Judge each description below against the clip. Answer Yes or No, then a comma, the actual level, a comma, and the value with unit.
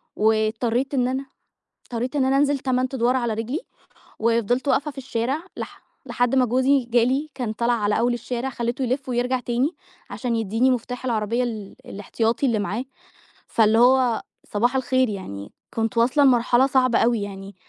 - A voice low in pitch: No, high, 245 Hz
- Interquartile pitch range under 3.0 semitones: Yes, narrow, 2.5 semitones